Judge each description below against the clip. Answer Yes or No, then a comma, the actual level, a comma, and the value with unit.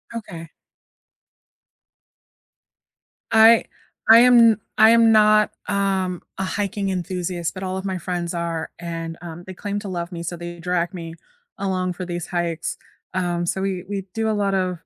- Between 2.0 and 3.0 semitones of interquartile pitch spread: Yes, average, 2.7 semitones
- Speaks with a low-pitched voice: No, medium, 185 Hz